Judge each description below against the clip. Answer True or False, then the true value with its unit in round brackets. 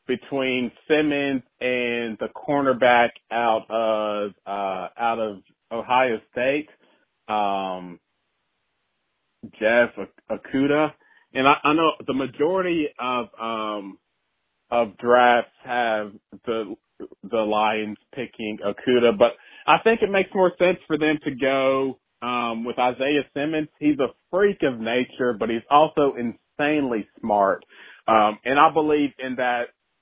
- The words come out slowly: True (125 wpm)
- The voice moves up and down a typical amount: True (4.5 semitones)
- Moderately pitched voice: False (125 Hz)